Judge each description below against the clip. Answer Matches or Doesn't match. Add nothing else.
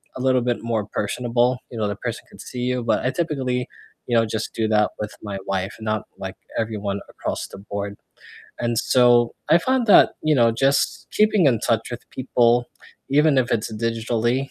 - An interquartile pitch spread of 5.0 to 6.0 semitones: Doesn't match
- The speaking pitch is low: Matches